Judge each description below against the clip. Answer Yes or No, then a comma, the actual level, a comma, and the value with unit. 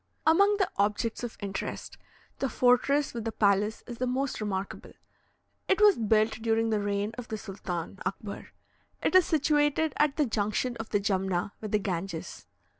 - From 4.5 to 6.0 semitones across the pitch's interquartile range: Yes, average, 5.2 semitones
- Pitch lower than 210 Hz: No, high, 225 Hz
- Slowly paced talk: No, average, 170 wpm